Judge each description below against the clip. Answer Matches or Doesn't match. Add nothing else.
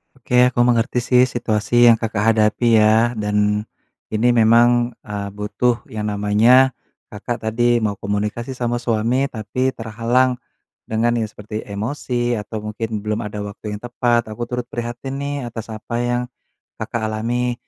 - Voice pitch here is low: Matches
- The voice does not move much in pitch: Matches